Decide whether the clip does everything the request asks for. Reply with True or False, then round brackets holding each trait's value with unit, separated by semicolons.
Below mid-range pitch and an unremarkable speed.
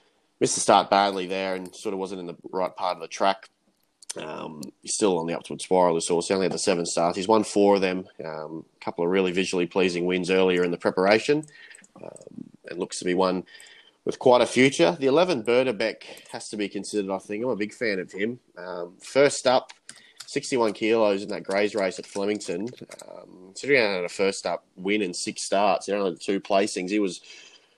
False (95 Hz; 215 wpm)